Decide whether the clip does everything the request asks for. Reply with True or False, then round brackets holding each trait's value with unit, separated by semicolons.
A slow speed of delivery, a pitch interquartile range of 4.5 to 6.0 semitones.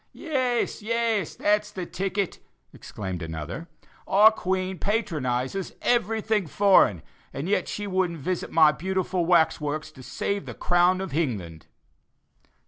True (130 wpm; 5.3 semitones)